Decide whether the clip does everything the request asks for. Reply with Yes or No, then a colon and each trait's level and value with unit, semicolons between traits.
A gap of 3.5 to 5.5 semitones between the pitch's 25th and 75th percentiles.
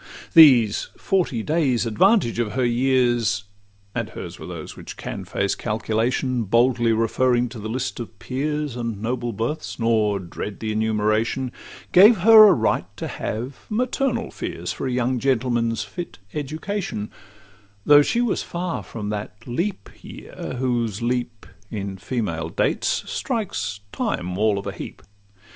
Yes: average, 4.2 semitones